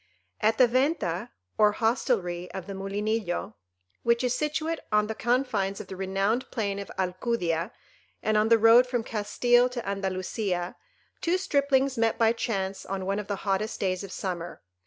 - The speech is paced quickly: No, average, 165 wpm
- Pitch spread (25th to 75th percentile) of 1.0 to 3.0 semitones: No, average, 3.9 semitones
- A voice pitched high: Yes, high, 210 Hz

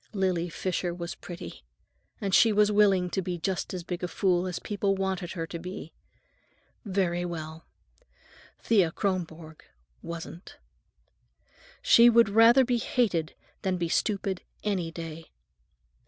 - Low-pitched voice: No, medium, 185 Hz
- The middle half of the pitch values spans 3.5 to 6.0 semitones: No, average, 2.9 semitones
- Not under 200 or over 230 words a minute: No, slow, 135 wpm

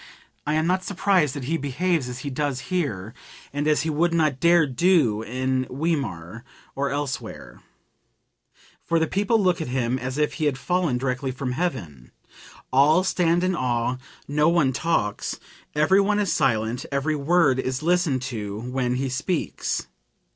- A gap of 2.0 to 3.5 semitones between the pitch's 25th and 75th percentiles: No, average, 4.8 semitones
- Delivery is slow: No, average, 160 wpm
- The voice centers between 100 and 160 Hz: Yes, medium, 140 Hz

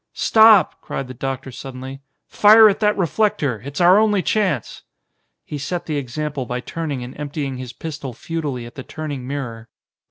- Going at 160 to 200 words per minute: Yes, average, 165 wpm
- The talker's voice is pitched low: No, medium, 145 Hz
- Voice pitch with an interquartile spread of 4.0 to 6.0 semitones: Yes, average, 5.2 semitones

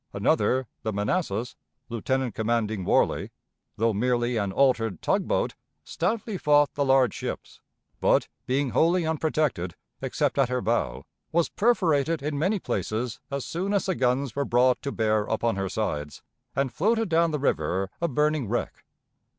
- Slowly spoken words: No, average, 155 wpm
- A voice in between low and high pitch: No, low, 130 Hz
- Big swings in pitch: Yes, wide, 5.9 semitones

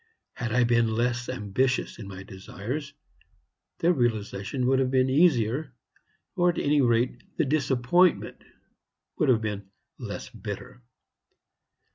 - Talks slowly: Yes, slow, 125 wpm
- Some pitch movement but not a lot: Yes, average, 3.2 semitones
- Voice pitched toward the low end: Yes, low, 125 Hz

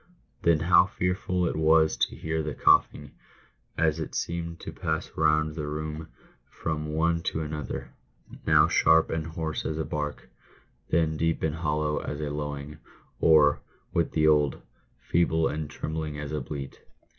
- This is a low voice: Yes, very low, 80 Hz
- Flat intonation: Yes, narrow, 1.3 semitones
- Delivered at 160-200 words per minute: Yes, average, 165 wpm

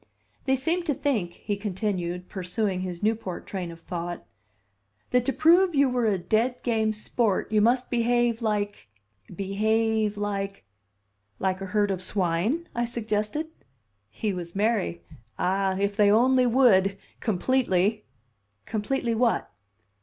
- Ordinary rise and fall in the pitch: Yes, average, 4.1 semitones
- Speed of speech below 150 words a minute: Yes, average, 140 wpm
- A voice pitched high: Yes, high, 210 Hz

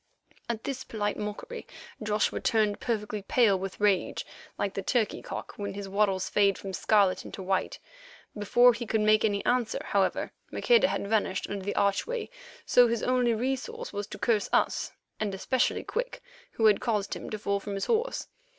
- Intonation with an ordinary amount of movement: Yes, average, 3.2 semitones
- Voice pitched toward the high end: Yes, high, 210 Hz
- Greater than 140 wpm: Yes, average, 180 wpm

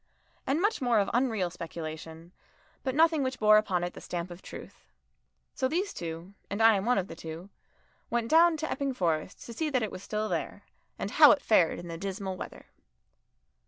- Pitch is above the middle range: Yes, high, 210 Hz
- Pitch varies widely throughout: Yes, wide, 6.8 semitones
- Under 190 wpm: No, average, 200 wpm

